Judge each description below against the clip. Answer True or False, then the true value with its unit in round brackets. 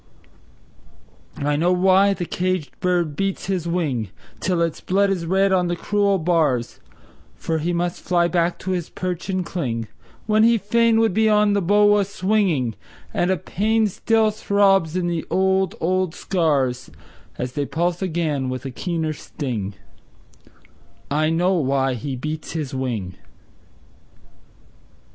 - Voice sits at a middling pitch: True (175 Hz)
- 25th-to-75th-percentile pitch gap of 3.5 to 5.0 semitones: True (4.3 semitones)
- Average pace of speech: True (150 wpm)